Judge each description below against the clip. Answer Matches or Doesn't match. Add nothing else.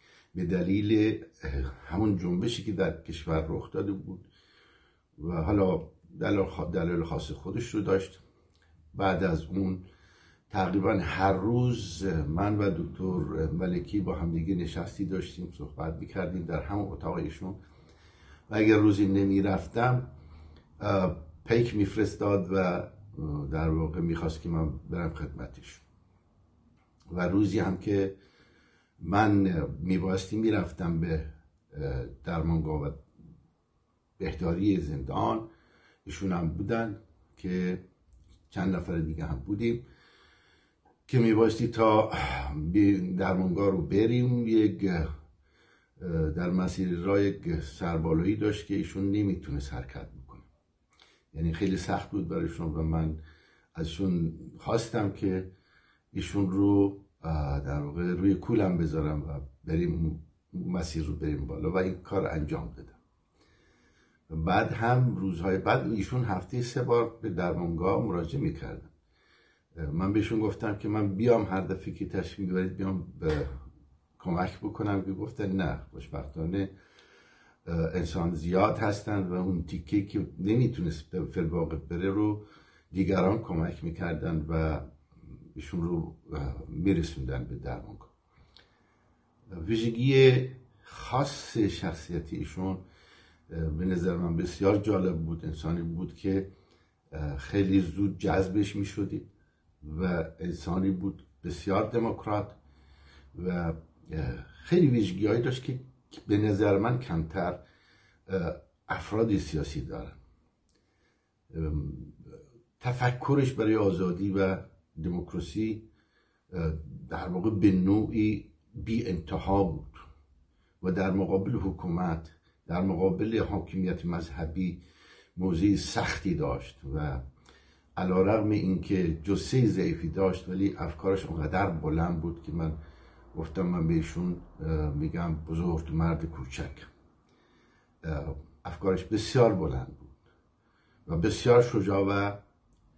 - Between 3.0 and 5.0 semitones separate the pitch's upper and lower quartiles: Matches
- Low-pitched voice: Matches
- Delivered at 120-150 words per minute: Doesn't match